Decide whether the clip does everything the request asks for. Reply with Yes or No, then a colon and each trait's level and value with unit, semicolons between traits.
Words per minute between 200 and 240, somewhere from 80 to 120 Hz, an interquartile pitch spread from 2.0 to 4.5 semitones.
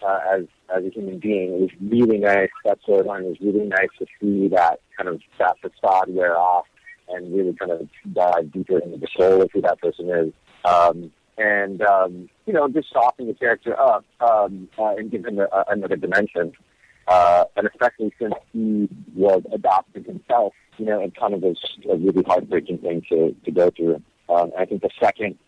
Yes: fast, 205 wpm; very low, 95 Hz; narrow, 2.5 semitones